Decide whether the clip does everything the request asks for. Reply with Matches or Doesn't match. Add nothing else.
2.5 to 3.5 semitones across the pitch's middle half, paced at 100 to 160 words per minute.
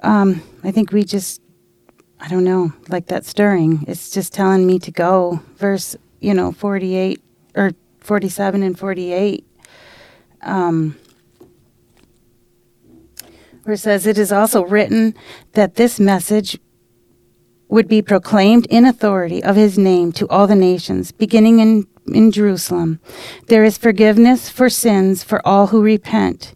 Matches